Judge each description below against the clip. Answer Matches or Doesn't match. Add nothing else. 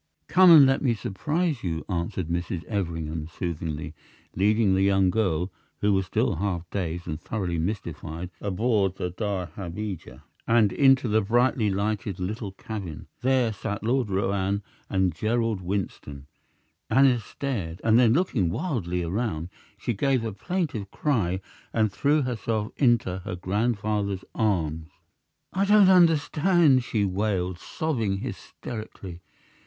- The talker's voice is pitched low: Matches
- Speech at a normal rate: Doesn't match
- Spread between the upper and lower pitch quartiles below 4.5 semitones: Doesn't match